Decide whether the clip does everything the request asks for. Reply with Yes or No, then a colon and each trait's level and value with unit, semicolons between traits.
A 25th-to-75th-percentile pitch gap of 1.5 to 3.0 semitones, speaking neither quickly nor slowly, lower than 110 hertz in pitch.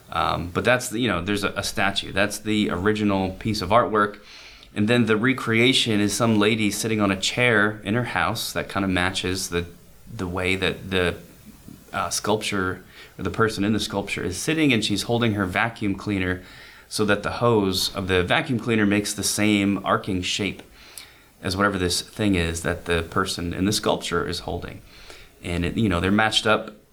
Yes: average, 2.7 semitones; average, 195 wpm; low, 100 Hz